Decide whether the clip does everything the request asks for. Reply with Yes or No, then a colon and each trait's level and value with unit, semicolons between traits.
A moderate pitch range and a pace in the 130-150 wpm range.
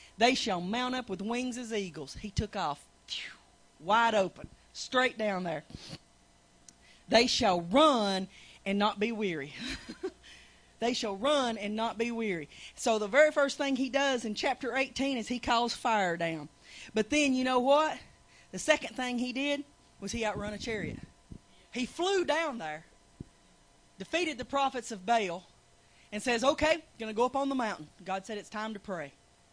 No: average, 4.6 semitones; average, 175 wpm